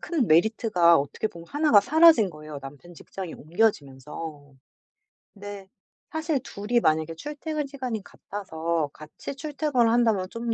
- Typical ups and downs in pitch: No, wide, 8.0 semitones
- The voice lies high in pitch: Yes, high, 205 Hz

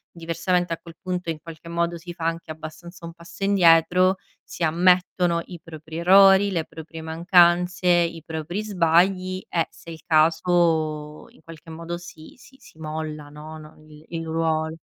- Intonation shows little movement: Yes, narrow, 1.8 semitones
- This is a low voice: No, medium, 170 Hz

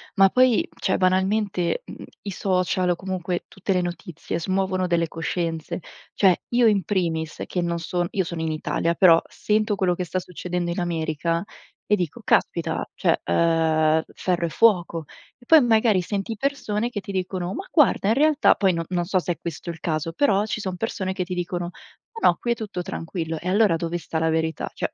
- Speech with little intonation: No, average, 3.2 semitones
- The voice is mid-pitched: Yes, medium, 180 Hz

